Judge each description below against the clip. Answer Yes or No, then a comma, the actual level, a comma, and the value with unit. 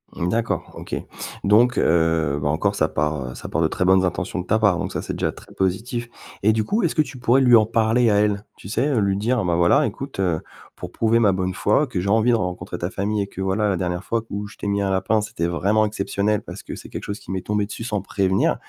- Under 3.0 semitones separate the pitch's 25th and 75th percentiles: No, average, 3.4 semitones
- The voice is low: Yes, low, 100 Hz